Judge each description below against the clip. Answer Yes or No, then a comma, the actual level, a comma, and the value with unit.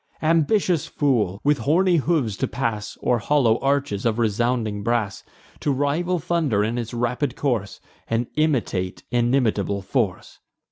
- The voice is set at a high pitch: No, low, 120 Hz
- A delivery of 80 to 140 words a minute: Yes, slow, 135 wpm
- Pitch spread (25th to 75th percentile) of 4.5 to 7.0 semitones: Yes, average, 5.1 semitones